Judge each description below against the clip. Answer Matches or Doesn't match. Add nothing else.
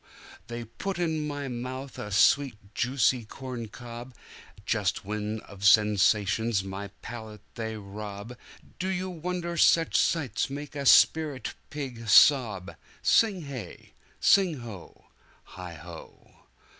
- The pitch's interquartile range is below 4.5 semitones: Doesn't match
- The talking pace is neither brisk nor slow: Doesn't match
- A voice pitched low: Matches